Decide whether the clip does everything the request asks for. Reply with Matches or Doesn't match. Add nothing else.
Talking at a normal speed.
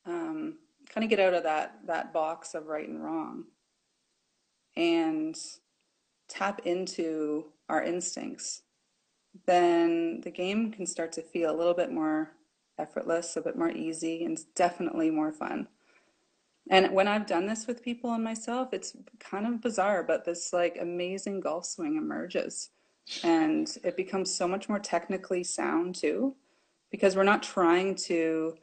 Matches